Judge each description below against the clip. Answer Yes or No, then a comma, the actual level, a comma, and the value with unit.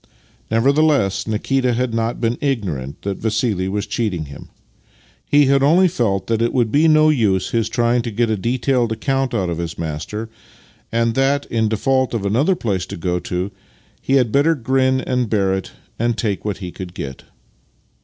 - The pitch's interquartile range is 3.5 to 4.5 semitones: No, average, 5.0 semitones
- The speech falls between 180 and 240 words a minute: Yes, average, 185 wpm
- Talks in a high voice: No, low, 115 Hz